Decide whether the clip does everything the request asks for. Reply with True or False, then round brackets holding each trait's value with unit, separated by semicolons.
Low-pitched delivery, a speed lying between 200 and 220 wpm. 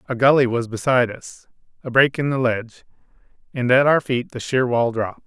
True (125 Hz; 205 wpm)